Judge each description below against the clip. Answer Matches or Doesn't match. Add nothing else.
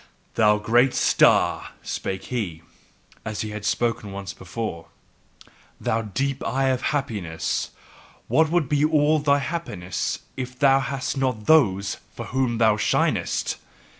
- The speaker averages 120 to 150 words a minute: Matches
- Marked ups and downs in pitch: Doesn't match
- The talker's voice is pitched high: Doesn't match